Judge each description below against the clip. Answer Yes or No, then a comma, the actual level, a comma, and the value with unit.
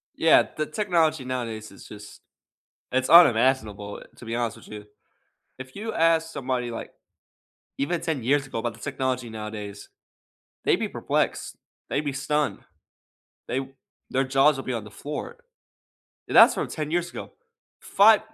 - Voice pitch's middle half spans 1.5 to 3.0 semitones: No, average, 4.9 semitones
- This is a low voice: Yes, low, 130 Hz